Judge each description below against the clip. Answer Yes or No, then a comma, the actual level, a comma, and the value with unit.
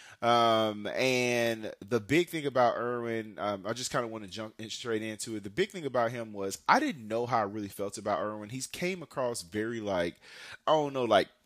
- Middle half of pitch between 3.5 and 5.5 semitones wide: No, average, 2.8 semitones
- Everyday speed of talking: No, fast, 220 wpm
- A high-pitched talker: No, low, 115 Hz